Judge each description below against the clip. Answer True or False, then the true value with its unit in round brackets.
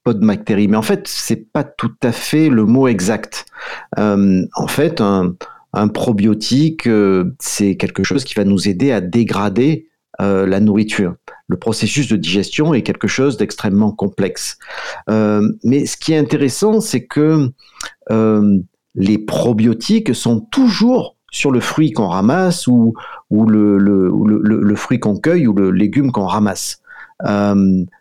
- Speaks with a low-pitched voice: True (110 Hz)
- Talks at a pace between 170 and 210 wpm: False (160 wpm)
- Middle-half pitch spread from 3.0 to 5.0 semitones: False (5.6 semitones)